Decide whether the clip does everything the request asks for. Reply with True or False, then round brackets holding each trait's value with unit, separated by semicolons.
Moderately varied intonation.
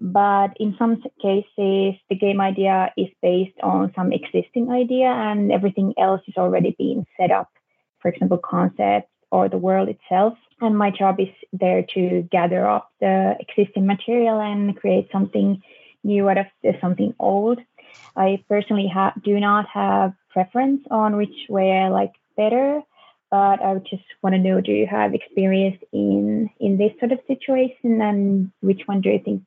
False (2.1 semitones)